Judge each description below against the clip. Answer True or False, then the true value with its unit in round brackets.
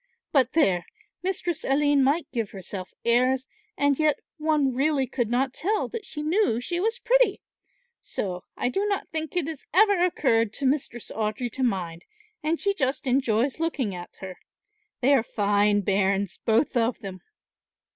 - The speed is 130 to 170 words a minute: True (165 wpm)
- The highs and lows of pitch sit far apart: True (6.5 semitones)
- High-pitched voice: True (265 Hz)